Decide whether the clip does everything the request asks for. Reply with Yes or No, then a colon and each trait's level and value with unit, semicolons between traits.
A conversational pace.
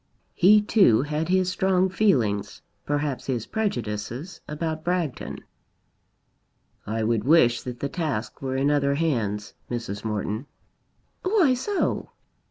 No: slow, 120 wpm